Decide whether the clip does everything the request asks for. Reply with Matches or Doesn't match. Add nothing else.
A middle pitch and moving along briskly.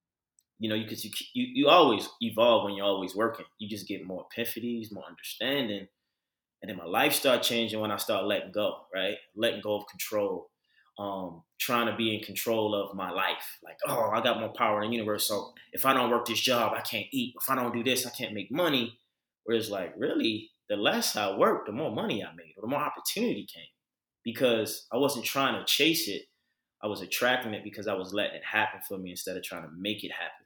Doesn't match